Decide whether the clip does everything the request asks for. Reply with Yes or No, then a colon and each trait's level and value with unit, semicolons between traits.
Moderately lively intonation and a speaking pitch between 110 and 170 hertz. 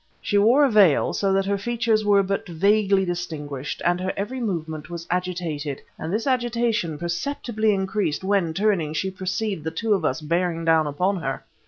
No: average, 4.3 semitones; high, 190 Hz